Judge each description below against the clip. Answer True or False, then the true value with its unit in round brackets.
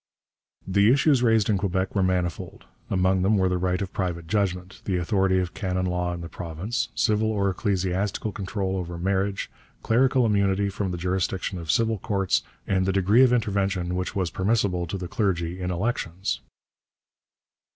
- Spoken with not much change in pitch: True (2.2 semitones)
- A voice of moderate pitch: False (95 Hz)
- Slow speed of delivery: False (170 wpm)